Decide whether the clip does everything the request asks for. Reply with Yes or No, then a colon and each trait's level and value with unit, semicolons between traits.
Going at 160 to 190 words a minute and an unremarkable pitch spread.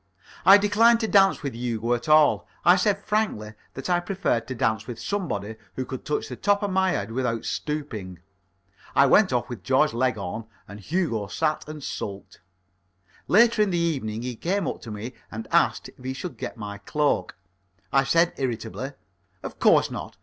No: average, 185 wpm; wide, 8.5 semitones